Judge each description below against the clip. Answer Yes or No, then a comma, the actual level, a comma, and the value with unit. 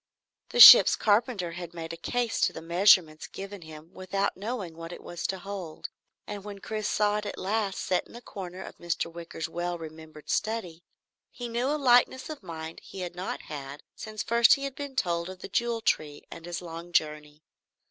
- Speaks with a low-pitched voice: No, medium, 185 Hz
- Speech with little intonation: No, average, 4.5 semitones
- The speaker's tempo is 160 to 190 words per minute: No, average, 200 wpm